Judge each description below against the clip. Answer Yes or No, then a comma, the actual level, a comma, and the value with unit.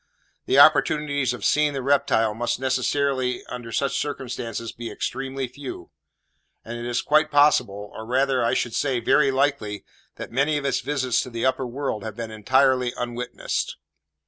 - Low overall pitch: Yes, low, 130 Hz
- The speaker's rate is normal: Yes, average, 165 wpm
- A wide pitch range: No, average, 2.9 semitones